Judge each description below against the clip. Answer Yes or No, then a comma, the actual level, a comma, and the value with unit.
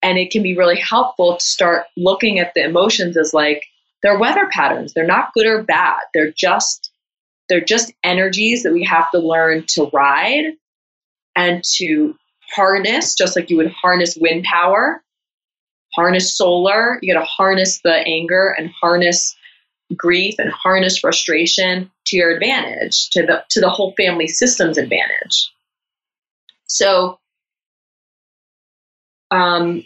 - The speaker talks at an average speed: Yes, average, 145 wpm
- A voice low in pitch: No, medium, 180 Hz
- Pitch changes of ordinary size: No, narrow, 2.3 semitones